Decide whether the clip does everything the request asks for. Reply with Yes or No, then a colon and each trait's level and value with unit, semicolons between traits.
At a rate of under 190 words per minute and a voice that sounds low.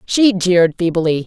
No: average, 140 wpm; medium, 180 Hz